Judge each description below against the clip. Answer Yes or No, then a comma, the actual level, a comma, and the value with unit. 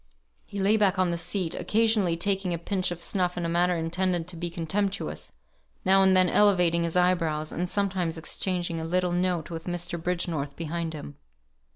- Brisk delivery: No, average, 185 wpm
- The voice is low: No, medium, 175 Hz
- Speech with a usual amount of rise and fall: No, narrow, 2.1 semitones